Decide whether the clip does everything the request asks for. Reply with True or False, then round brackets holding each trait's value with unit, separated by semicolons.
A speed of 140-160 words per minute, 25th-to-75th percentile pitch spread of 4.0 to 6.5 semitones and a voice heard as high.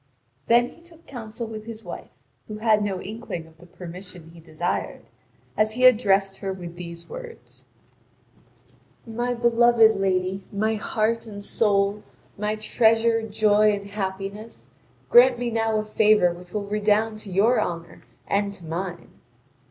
False (150 wpm; 3.0 semitones; 210 Hz)